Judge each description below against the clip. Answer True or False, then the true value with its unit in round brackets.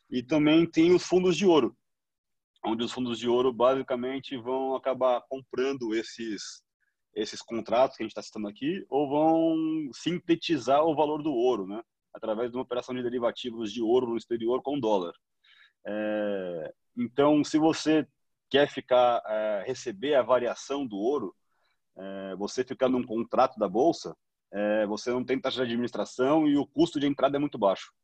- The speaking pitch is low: True (130 Hz)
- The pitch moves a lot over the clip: False (4.3 semitones)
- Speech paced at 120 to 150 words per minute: False (170 wpm)